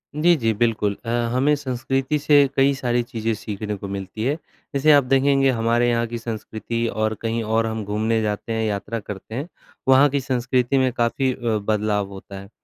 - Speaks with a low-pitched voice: Yes, low, 115 Hz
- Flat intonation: No, average, 3.5 semitones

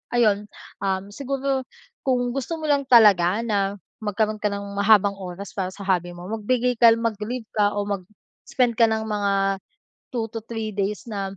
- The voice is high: Yes, high, 210 Hz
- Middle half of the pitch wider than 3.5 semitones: No, average, 3.0 semitones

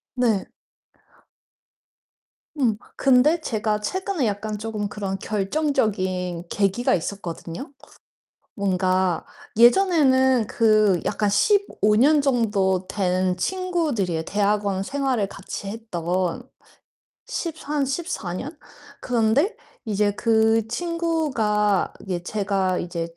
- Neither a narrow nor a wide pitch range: No, wide, 5.8 semitones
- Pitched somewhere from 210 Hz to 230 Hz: Yes, high, 215 Hz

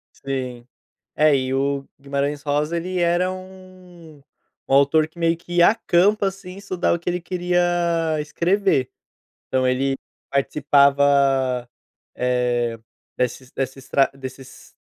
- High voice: No, medium, 145 Hz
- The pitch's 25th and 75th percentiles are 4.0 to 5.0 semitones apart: Yes, average, 4.7 semitones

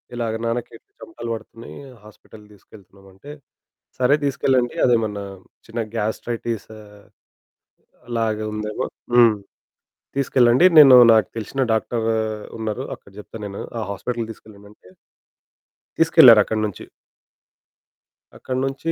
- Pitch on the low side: Yes, low, 115 Hz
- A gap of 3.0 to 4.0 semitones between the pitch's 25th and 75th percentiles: No, narrow, 2.6 semitones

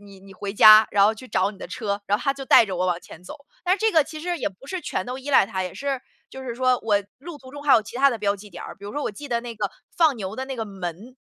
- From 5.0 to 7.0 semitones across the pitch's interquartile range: Yes, average, 5.3 semitones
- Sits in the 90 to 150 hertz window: No, high, 230 Hz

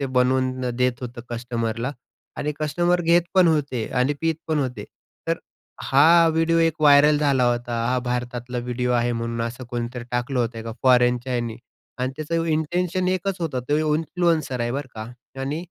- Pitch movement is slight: No, average, 4.2 semitones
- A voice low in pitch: Yes, low, 130 Hz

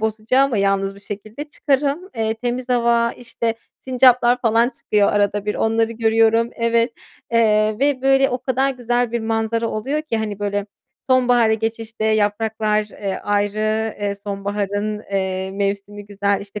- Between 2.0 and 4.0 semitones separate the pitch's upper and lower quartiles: Yes, average, 2.7 semitones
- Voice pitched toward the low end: No, high, 220 Hz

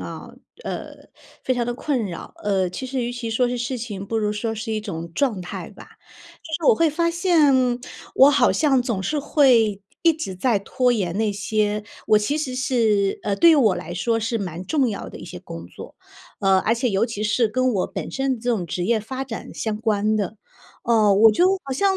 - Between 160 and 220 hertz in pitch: No, high, 230 Hz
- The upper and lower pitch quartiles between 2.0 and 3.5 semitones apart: No, average, 4.1 semitones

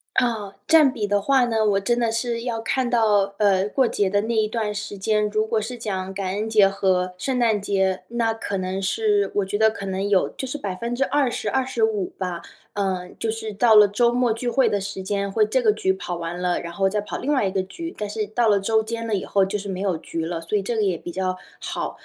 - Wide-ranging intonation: No, average, 3.2 semitones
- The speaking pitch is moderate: No, high, 210 Hz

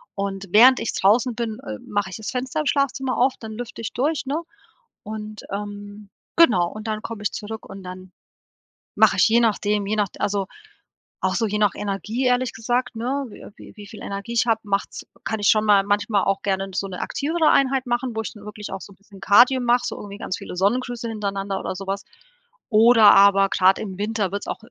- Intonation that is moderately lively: Yes, average, 3.3 semitones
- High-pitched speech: Yes, high, 210 Hz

